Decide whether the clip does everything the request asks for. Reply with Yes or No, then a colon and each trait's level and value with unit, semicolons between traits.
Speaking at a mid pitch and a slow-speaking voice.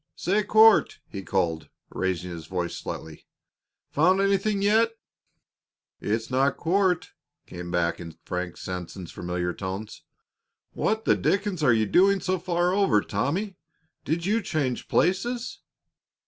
Yes: medium, 150 Hz; slow, 130 wpm